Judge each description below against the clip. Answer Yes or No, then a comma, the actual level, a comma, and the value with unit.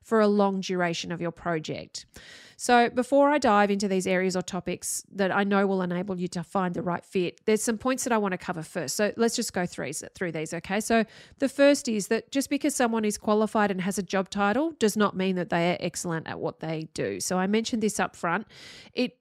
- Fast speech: Yes, fast, 240 wpm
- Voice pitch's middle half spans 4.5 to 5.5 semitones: No, average, 4.0 semitones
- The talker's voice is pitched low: No, high, 200 Hz